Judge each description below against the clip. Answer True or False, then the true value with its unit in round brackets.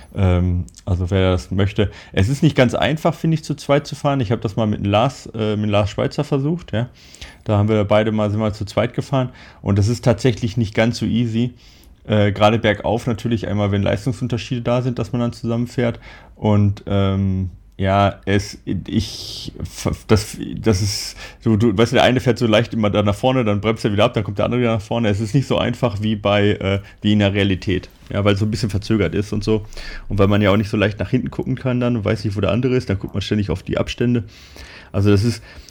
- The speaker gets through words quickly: True (240 wpm)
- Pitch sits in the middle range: False (110 Hz)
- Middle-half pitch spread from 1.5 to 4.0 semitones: True (3.0 semitones)